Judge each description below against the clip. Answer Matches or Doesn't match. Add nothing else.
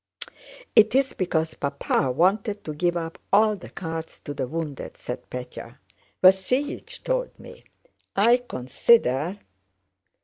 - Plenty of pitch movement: Matches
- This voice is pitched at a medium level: Matches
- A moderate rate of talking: Doesn't match